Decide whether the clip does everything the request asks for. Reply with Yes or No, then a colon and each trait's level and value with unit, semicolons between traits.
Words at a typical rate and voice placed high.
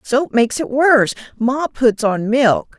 Yes: average, 150 wpm; high, 245 Hz